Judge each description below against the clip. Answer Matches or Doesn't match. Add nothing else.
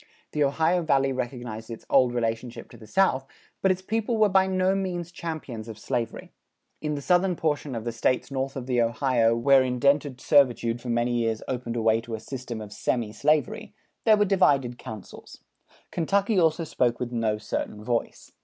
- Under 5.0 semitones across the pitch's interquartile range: Doesn't match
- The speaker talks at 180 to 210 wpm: Matches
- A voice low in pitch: Matches